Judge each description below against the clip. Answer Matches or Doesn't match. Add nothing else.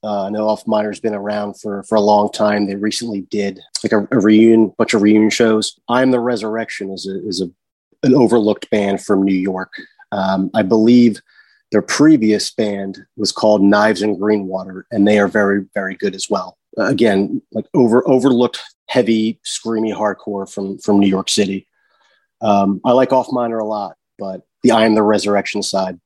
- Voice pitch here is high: Doesn't match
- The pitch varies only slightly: Matches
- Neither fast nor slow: Matches